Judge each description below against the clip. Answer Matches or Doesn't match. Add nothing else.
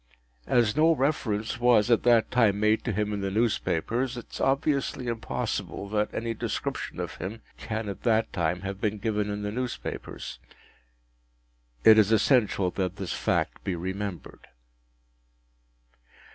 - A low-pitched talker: Matches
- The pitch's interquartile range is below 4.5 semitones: Matches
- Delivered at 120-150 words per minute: Matches